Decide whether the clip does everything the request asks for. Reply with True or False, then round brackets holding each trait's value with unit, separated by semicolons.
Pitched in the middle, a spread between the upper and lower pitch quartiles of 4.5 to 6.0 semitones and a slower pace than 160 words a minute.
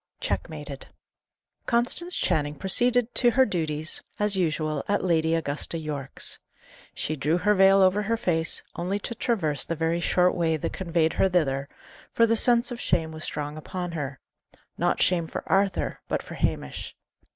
False (175 Hz; 4.8 semitones; 165 wpm)